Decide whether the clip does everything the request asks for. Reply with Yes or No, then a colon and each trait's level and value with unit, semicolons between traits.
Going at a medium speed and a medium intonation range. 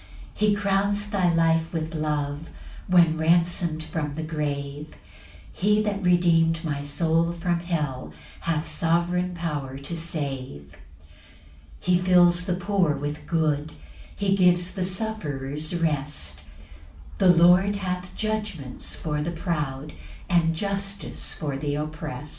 No: slow, 130 wpm; average, 3.2 semitones